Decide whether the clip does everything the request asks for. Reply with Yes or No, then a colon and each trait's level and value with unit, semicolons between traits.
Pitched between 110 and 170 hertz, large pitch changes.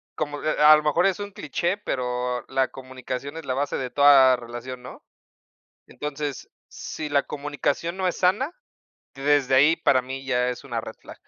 No: medium, 140 Hz; average, 3.1 semitones